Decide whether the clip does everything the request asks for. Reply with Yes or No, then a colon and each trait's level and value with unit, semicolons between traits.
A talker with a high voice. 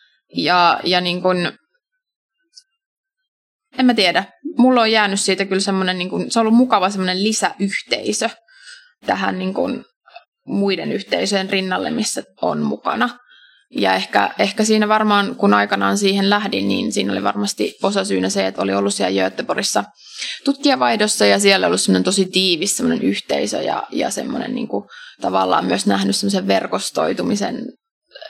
Yes: high, 195 Hz